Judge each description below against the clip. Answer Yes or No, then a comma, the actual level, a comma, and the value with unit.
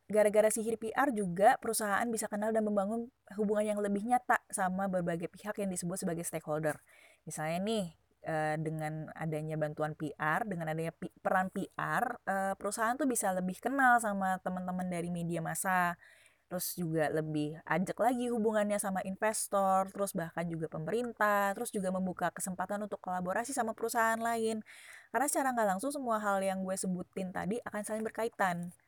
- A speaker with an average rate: No, fast, 155 wpm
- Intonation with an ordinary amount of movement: Yes, average, 4.0 semitones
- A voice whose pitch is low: No, high, 195 Hz